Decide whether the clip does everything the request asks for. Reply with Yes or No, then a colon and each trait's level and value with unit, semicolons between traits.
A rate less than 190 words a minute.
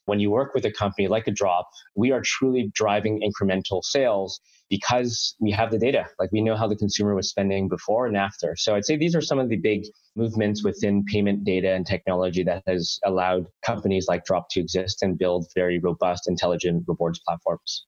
No: fast, 205 wpm